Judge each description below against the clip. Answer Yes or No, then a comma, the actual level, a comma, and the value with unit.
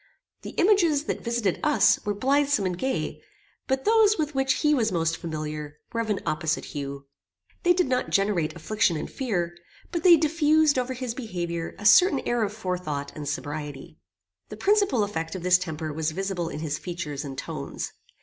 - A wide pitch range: Yes, wide, 8.9 semitones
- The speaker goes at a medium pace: Yes, average, 180 wpm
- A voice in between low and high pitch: No, high, 200 Hz